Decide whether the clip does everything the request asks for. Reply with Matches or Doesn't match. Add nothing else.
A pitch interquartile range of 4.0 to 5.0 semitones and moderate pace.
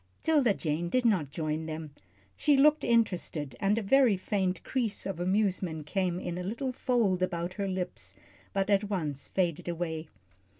Matches